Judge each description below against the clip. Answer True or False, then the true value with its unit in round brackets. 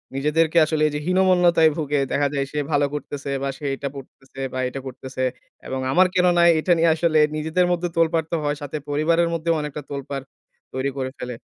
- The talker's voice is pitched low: False (150 Hz)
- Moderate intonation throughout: True (3.3 semitones)